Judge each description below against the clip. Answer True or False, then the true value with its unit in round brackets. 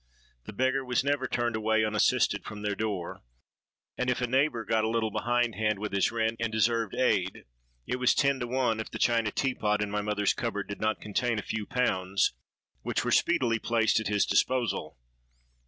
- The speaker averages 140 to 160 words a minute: False (200 wpm)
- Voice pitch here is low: True (110 Hz)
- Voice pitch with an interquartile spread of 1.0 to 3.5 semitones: True (2.7 semitones)